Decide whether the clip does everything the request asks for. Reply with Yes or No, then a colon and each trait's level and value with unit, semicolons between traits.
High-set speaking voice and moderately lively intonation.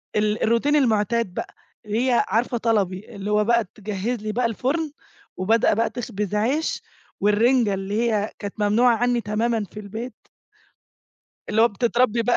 No: high, 225 Hz; narrow, 2.3 semitones